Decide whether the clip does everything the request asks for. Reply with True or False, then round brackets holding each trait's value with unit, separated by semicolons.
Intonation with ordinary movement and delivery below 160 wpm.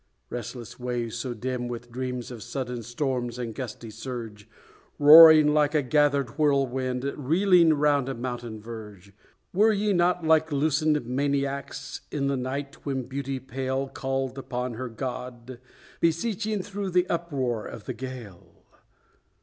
True (3.5 semitones; 140 wpm)